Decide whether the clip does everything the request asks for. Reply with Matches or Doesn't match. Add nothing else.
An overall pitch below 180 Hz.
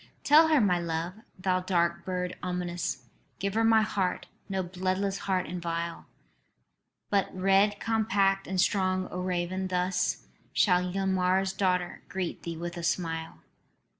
Doesn't match